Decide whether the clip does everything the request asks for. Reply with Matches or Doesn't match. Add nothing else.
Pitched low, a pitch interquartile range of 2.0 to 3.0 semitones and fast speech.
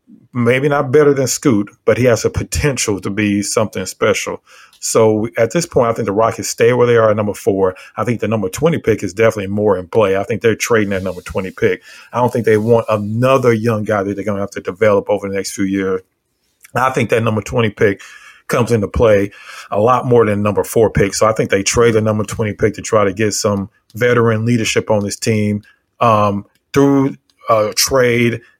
Matches